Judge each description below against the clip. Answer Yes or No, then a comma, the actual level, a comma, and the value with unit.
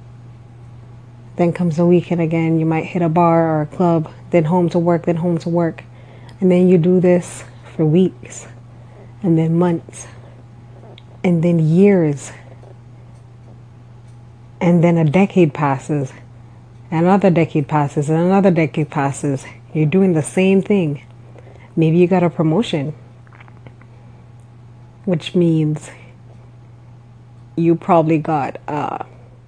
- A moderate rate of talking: No, slow, 130 wpm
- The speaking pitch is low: No, medium, 145 Hz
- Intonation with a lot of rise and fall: Yes, wide, 6.2 semitones